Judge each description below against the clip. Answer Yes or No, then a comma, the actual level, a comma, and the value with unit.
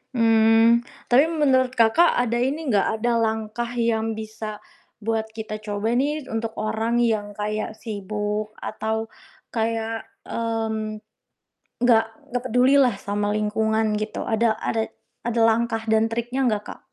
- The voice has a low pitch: No, high, 225 Hz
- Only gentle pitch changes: Yes, narrow, 1.5 semitones